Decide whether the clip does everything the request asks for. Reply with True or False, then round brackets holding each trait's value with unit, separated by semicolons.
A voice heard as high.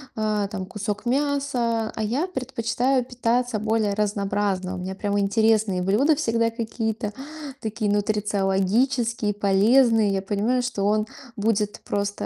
True (215 Hz)